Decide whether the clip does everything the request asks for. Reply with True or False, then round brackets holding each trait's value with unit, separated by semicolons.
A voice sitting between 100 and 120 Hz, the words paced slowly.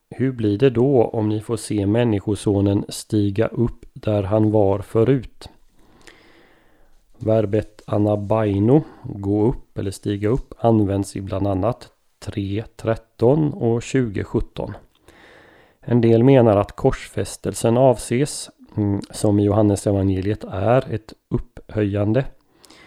True (110 Hz; 110 wpm)